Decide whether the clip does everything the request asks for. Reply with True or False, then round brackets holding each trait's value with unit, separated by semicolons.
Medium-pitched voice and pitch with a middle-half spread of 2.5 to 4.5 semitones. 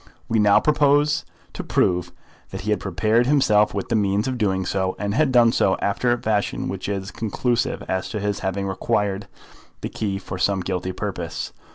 False (105 Hz; 3.2 semitones)